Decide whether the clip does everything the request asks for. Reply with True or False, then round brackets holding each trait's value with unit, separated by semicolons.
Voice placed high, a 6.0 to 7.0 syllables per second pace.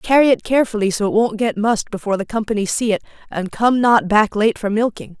True (215 Hz; 6.2 syllables/s)